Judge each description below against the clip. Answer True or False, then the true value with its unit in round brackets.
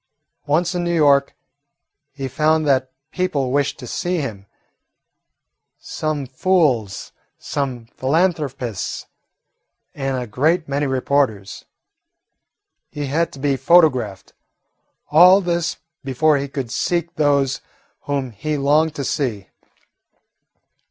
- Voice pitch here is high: False (140 Hz)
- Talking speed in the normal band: False (110 wpm)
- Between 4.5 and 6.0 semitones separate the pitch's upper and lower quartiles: False (3.4 semitones)